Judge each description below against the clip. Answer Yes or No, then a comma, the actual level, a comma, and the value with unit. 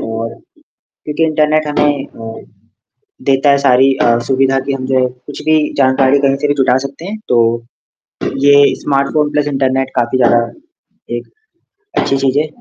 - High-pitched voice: No, low, 135 Hz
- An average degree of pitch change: No, narrow, 2.2 semitones